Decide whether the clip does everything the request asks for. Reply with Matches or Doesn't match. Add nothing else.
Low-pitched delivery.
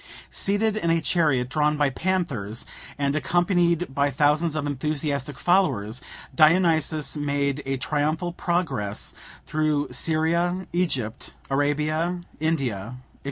Doesn't match